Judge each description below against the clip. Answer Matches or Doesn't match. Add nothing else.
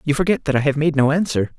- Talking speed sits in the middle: Doesn't match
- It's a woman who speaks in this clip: Doesn't match